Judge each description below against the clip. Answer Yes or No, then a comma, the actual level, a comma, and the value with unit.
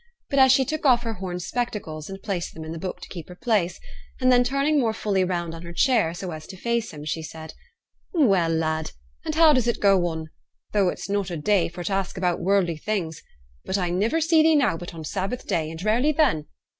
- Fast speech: Yes, fast, 230 wpm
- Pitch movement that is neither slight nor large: No, wide, 6.2 semitones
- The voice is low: No, high, 190 Hz